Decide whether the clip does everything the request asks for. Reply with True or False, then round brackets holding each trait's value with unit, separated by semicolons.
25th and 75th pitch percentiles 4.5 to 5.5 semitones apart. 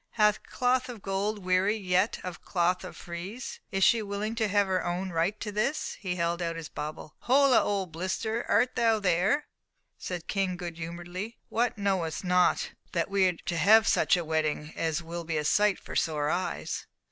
False (3.8 semitones)